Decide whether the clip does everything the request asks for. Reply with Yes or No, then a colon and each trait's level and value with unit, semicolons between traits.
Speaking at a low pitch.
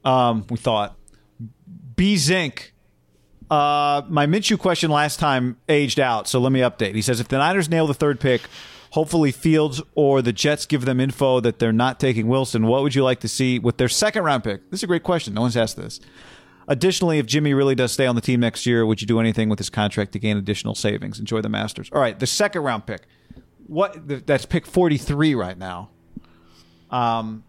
Yes: low, 130 Hz